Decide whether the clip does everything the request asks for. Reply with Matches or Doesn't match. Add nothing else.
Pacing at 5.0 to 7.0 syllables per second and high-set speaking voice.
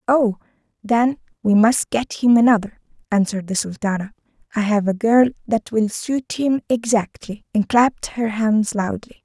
Doesn't match